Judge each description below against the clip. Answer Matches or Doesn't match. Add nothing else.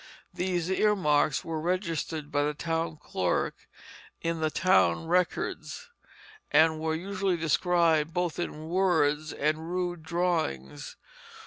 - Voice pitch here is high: Doesn't match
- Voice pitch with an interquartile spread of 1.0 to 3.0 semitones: Matches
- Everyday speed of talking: Doesn't match